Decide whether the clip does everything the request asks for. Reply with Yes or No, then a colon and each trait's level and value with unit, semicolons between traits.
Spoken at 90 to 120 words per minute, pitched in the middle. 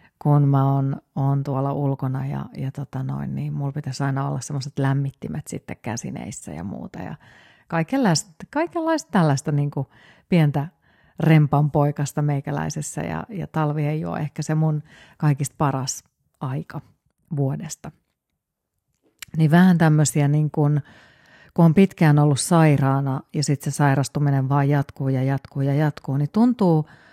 No: average, 145 wpm; medium, 145 Hz